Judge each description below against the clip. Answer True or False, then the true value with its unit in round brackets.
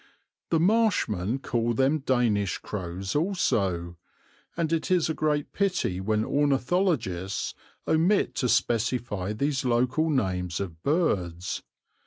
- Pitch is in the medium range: False (125 Hz)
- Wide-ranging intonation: True (8.3 semitones)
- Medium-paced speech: False (115 wpm)